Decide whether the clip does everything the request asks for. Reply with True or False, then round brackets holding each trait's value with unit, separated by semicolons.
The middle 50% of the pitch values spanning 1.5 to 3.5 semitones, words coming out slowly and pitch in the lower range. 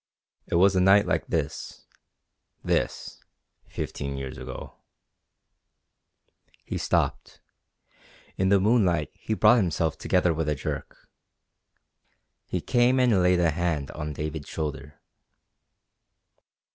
False (4.5 semitones; 110 wpm; 85 Hz)